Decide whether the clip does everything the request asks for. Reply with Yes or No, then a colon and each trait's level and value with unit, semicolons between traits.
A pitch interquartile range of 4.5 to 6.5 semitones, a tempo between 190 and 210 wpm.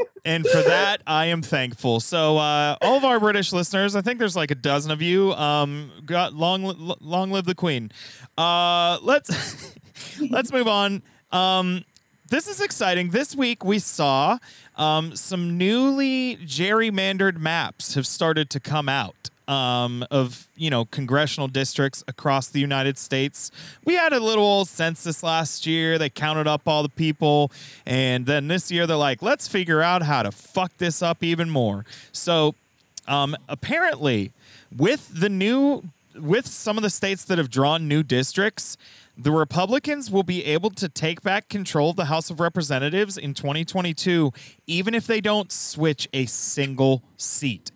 No: average, 5.2 semitones; average, 165 wpm